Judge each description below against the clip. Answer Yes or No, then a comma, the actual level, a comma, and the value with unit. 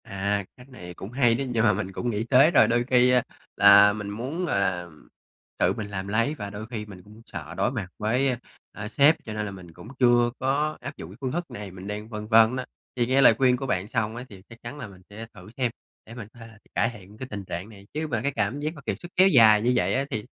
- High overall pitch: No, low, 110 Hz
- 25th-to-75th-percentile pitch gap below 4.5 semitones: Yes, average, 3.8 semitones